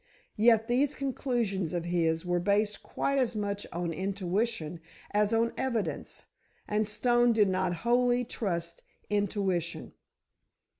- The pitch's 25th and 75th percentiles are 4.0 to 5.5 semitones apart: Yes, average, 4.9 semitones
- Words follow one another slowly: Yes, slow, 120 wpm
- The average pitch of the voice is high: Yes, high, 205 Hz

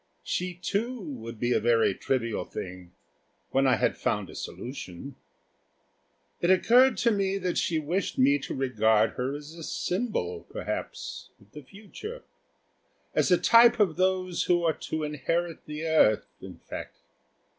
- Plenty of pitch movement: Yes, wide, 7.0 semitones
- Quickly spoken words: No, average, 155 wpm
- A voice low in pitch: No, medium, 160 Hz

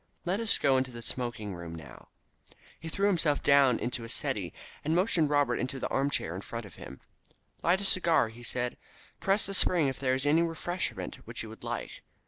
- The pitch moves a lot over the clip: Yes, wide, 5.9 semitones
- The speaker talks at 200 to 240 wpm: Yes, fast, 205 wpm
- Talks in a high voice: No, medium, 140 Hz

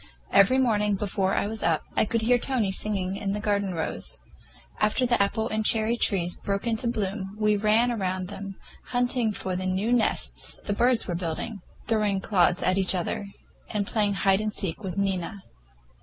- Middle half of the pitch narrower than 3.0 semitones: Yes, narrow, 2.6 semitones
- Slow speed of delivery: No, average, 185 wpm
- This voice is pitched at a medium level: No, high, 205 Hz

